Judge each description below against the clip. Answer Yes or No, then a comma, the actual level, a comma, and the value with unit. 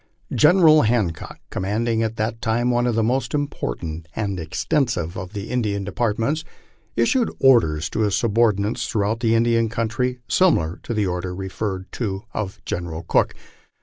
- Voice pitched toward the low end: Yes, low, 110 Hz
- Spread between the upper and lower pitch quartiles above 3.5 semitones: Yes, average, 3.9 semitones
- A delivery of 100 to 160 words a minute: Yes, average, 150 wpm